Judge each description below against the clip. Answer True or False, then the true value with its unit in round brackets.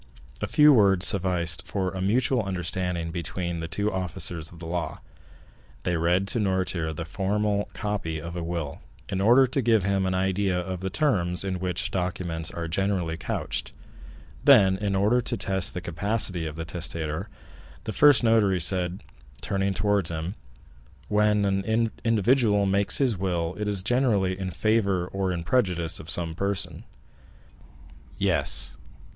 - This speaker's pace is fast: False (160 wpm)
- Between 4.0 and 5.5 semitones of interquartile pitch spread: False (3.0 semitones)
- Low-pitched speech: True (95 Hz)